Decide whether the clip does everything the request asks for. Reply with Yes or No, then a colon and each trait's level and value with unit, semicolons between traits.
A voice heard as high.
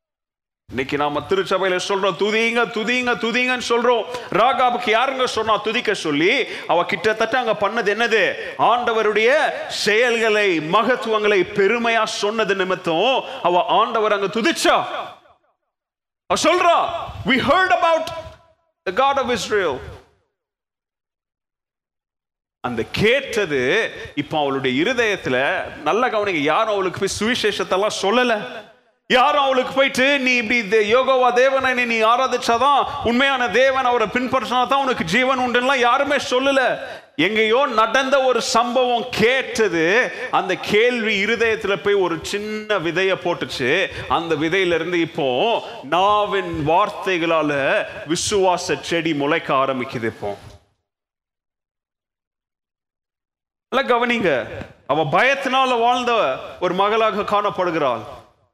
Yes: high, 220 Hz